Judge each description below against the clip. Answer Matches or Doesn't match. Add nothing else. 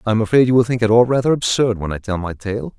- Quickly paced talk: Matches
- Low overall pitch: Matches